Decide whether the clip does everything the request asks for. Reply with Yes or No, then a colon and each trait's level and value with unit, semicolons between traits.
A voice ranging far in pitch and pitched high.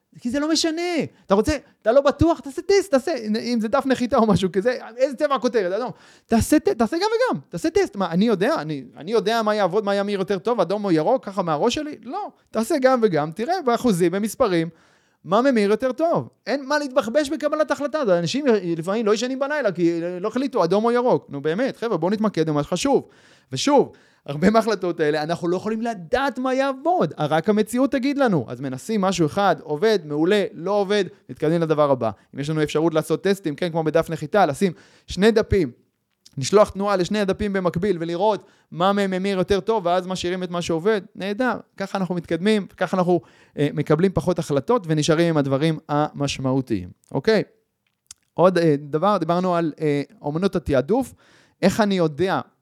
Yes: wide, 6.2 semitones; high, 200 Hz